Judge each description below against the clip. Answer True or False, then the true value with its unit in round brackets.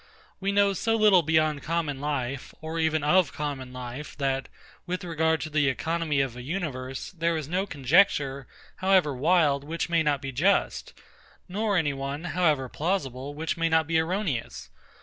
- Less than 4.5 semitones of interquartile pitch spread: True (4.0 semitones)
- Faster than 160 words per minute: True (170 wpm)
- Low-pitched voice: False (155 Hz)